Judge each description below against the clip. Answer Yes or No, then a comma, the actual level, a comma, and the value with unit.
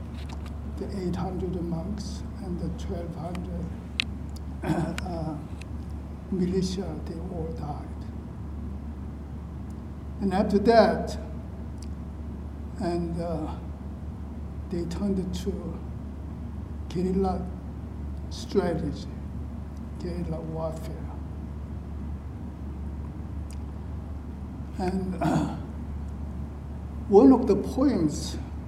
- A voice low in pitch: Yes, very low, 80 Hz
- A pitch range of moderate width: No, narrow, 2.1 semitones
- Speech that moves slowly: Yes, slow, 60 wpm